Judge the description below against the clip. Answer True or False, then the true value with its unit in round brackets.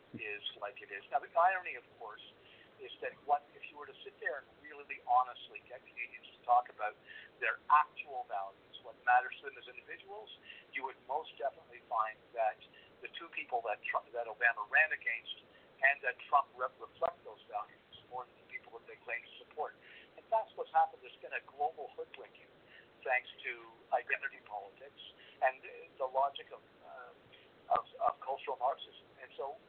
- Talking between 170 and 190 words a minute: True (185 wpm)